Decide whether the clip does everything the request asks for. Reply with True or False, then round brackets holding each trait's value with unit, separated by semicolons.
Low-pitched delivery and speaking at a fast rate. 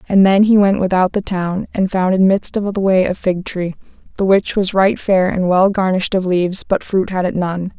False (190 Hz; 245 wpm)